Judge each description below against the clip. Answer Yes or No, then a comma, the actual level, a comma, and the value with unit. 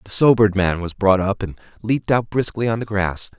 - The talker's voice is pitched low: Yes, low, 105 Hz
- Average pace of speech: No, fast, 230 wpm